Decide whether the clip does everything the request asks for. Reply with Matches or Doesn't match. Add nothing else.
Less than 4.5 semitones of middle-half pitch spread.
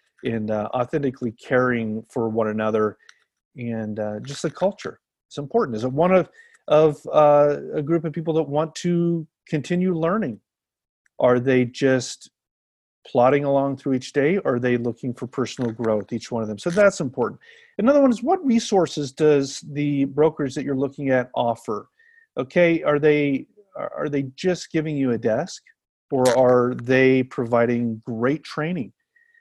Doesn't match